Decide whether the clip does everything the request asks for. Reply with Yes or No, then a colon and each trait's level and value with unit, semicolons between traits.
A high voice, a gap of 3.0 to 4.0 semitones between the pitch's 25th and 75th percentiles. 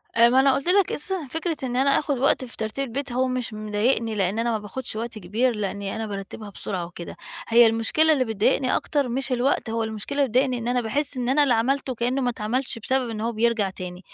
Yes: high, 240 Hz; average, 3.5 semitones